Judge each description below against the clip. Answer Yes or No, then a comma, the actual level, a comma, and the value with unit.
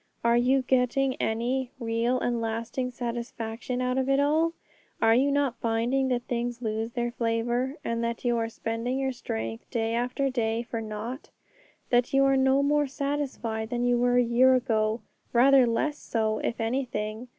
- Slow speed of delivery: No, average, 175 wpm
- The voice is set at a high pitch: Yes, high, 240 Hz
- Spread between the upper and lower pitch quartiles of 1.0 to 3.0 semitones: Yes, narrow, 2.4 semitones